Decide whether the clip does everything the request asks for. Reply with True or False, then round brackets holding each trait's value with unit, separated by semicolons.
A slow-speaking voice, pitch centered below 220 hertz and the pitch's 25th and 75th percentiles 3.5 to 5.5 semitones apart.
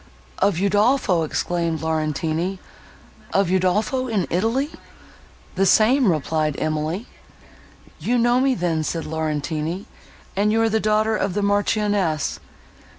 True (120 wpm; 190 Hz; 5.2 semitones)